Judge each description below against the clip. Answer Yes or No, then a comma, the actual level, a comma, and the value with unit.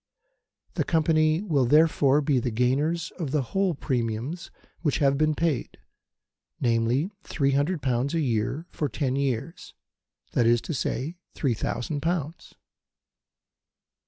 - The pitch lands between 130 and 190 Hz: Yes, medium, 140 Hz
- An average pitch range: Yes, average, 4.2 semitones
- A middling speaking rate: No, slow, 125 wpm